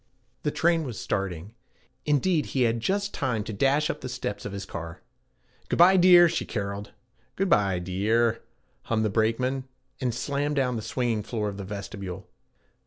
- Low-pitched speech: Yes, low, 115 Hz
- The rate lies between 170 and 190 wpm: Yes, average, 175 wpm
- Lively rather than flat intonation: Yes, wide, 6.1 semitones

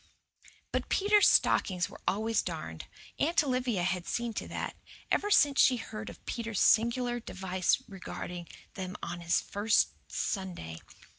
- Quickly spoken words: No, average, 140 wpm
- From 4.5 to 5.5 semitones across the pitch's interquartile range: Yes, average, 5.1 semitones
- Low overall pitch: No, high, 215 Hz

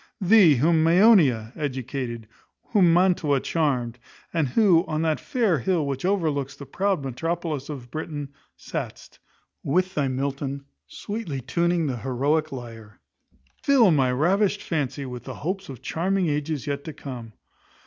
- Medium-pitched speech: Yes, medium, 150 Hz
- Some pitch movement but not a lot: Yes, average, 4.7 semitones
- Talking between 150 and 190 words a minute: No, average, 140 wpm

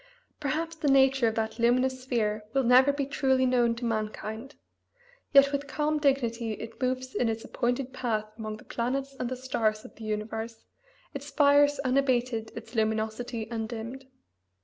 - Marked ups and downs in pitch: No, average, 3.3 semitones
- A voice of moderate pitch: No, high, 245 Hz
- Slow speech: No, average, 160 wpm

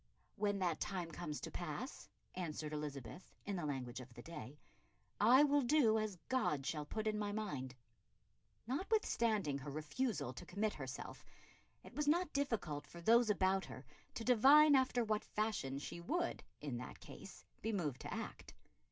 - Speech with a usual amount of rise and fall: No, wide, 7.9 semitones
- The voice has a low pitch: No, high, 195 Hz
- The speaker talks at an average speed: Yes, average, 165 wpm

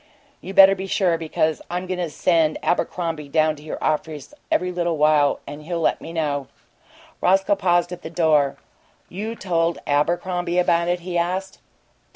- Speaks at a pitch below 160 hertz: No, medium, 170 Hz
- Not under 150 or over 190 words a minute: Yes, average, 170 wpm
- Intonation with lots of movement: No, narrow, 2.6 semitones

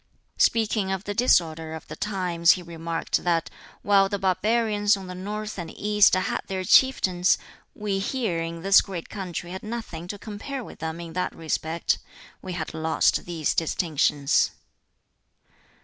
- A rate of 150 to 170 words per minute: Yes, average, 155 wpm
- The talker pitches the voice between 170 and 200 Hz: Yes, medium, 185 Hz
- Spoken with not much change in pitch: No, average, 3.7 semitones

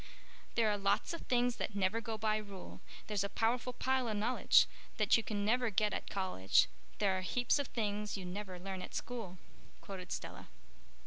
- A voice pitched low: No, high, 210 Hz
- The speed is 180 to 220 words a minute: Yes, average, 185 wpm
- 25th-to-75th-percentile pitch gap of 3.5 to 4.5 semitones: No, average, 3.1 semitones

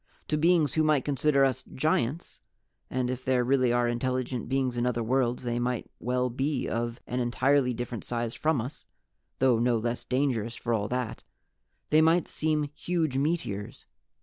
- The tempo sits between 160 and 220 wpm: Yes, average, 170 wpm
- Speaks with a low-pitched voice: Yes, low, 125 Hz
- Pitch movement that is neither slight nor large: Yes, average, 3.0 semitones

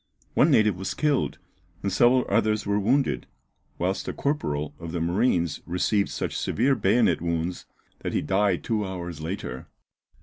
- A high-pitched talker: No, very low, 95 Hz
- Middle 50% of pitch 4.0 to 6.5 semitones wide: Yes, average, 4.3 semitones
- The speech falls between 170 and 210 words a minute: No, average, 155 wpm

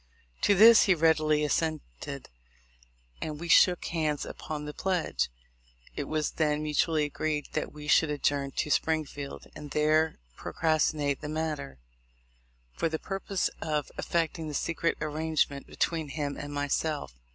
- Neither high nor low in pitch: Yes, medium, 155 Hz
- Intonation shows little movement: Yes, narrow, 1.5 semitones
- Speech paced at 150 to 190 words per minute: No, average, 140 wpm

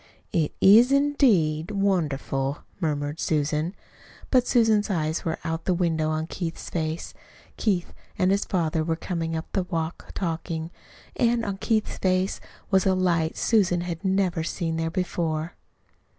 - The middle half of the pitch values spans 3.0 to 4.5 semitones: Yes, average, 3.3 semitones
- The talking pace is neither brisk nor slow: Yes, average, 145 wpm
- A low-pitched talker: No, medium, 170 Hz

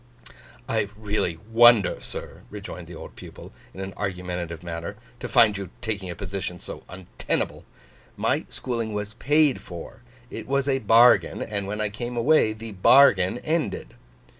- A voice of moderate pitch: No, low, 105 Hz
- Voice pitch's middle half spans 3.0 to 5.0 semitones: Yes, average, 4.1 semitones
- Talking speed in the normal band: Yes, average, 155 wpm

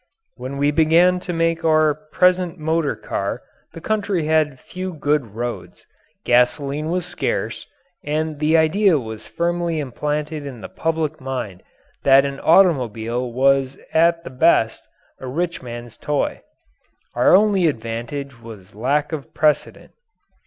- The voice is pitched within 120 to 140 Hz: No, medium, 150 Hz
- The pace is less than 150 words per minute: Yes, slow, 135 wpm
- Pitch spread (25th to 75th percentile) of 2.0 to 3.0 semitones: No, average, 4.4 semitones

